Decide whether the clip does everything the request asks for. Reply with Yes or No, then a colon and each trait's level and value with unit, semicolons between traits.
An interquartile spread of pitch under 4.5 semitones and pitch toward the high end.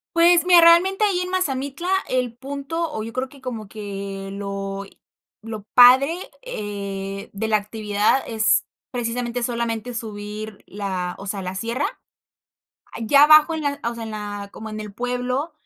No: average, 5.1 semitones; high, 230 Hz